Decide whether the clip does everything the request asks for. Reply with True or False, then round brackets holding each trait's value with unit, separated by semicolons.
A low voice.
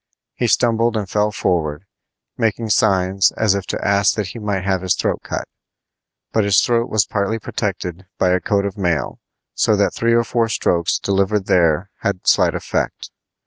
True (100 Hz)